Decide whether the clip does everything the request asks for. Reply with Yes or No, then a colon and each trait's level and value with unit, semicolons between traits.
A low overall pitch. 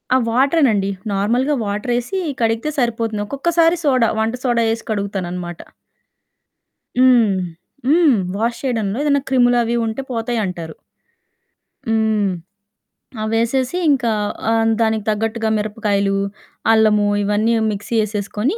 No: high, 225 Hz